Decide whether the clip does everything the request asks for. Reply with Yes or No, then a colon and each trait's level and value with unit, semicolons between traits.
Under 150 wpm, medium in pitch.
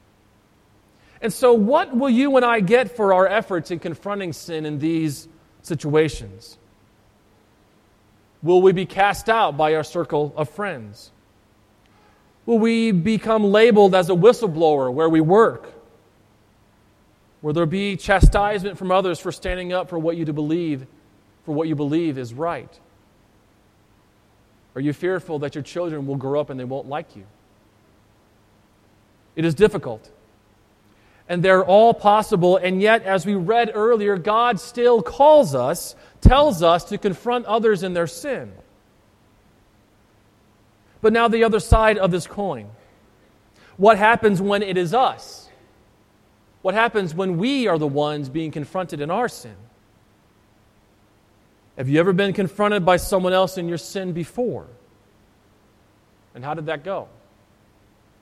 Yes: average, 140 wpm; medium, 155 Hz